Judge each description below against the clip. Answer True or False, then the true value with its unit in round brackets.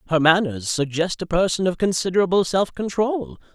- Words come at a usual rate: True (150 wpm)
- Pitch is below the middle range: False (175 Hz)